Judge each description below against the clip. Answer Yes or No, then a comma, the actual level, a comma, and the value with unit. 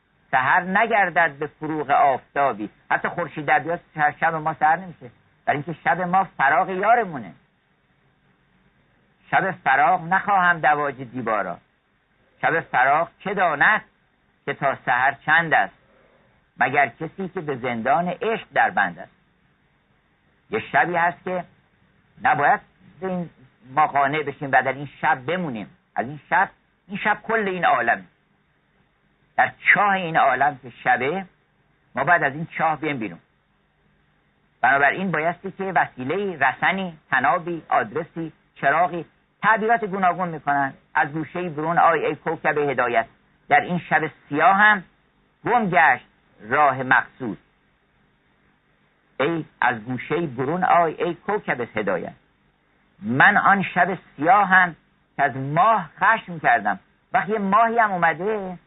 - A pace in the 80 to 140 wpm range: Yes, average, 130 wpm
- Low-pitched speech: No, medium, 165 Hz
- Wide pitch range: No, average, 4.4 semitones